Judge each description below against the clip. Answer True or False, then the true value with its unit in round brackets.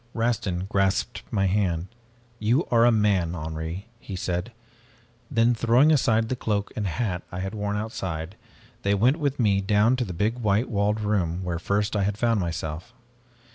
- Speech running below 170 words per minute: False (175 wpm)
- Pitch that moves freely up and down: False (3.8 semitones)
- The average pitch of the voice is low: True (105 Hz)